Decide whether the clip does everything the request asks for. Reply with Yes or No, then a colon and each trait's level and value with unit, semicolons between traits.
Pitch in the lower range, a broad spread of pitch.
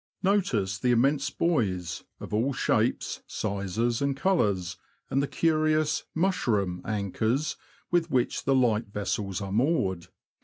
Yes: low, 120 Hz; wide, 7.5 semitones